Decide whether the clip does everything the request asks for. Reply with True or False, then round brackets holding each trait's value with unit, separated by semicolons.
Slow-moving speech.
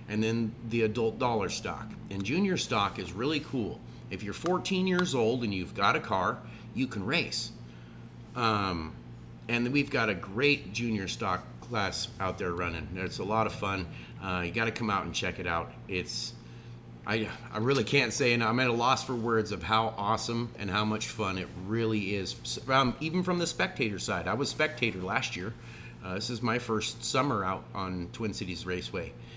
False (200 wpm)